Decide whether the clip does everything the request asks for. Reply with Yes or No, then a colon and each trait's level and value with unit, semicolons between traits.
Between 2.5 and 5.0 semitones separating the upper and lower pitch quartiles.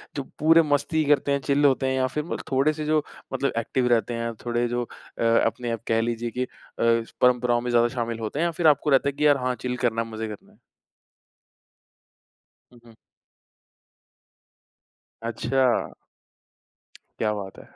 Yes: average, 3.3 semitones